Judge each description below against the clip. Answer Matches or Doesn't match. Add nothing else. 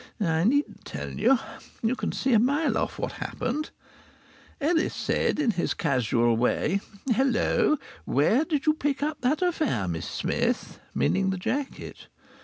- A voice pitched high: Matches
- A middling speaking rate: Matches